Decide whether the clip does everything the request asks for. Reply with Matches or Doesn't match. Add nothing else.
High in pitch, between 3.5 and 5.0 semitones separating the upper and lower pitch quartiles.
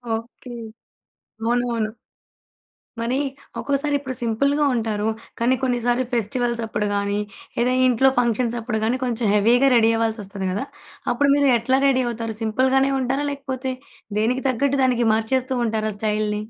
Doesn't match